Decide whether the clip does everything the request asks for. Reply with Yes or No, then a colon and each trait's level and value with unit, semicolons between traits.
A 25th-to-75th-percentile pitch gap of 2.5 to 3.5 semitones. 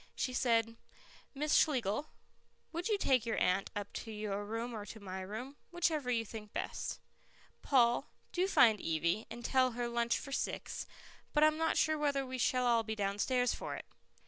No: average, 4.3 semitones